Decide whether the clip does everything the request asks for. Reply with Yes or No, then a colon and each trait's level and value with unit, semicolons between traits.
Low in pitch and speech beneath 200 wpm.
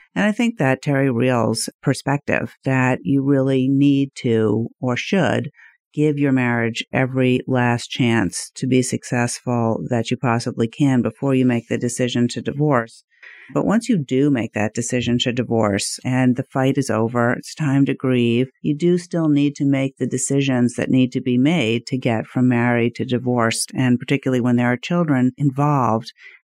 Yes: low, 125 Hz; average, 175 wpm